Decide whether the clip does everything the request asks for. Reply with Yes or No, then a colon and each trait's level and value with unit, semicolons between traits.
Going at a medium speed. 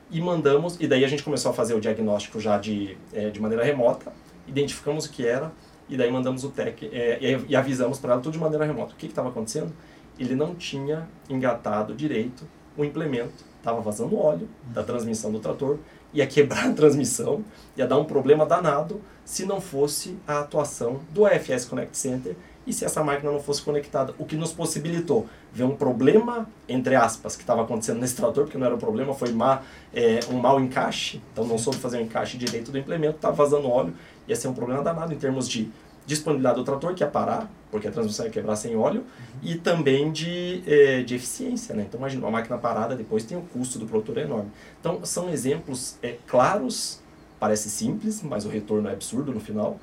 No: fast, 210 wpm